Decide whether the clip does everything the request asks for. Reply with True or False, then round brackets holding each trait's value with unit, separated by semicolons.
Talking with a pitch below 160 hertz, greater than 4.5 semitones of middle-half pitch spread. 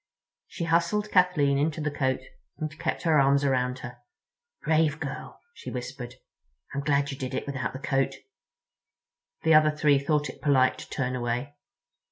False (140 Hz; 2.7 semitones)